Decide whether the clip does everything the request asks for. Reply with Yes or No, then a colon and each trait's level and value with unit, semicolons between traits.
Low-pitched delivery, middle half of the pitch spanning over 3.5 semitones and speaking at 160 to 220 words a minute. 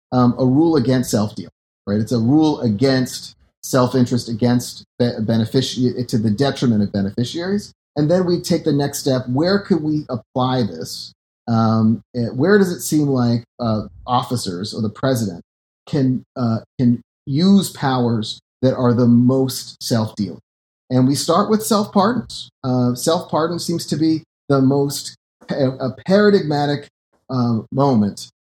No: low, 130 Hz; average, 4.3 semitones; average, 145 wpm